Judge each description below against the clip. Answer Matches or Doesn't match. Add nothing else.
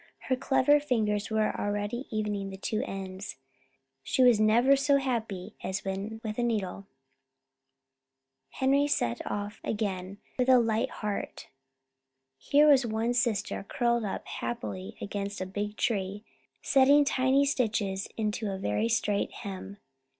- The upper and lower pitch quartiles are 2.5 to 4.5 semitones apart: Matches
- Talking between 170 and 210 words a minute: Doesn't match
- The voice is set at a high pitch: Matches